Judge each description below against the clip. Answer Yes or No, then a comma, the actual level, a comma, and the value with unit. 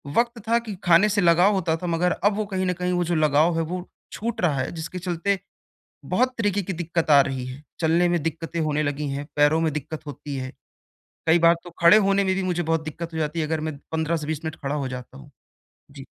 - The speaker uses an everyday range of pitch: Yes, average, 3.0 semitones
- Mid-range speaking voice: Yes, medium, 165 Hz